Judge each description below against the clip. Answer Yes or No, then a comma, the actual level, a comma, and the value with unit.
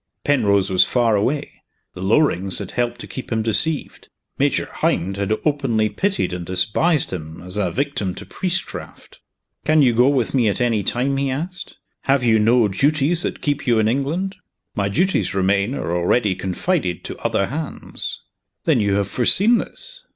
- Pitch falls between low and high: No, low, 120 Hz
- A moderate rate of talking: Yes, average, 175 wpm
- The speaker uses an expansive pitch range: Yes, wide, 6.5 semitones